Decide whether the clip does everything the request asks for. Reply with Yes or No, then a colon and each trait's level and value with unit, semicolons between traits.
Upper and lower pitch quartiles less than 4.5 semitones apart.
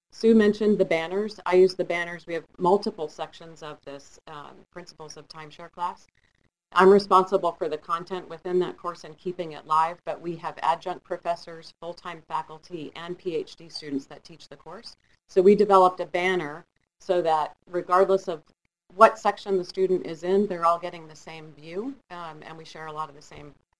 Yes: average, 2.7 semitones